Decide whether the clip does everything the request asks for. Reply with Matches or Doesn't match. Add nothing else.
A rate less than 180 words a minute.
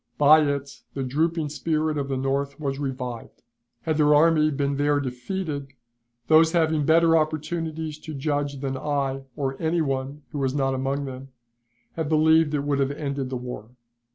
Matches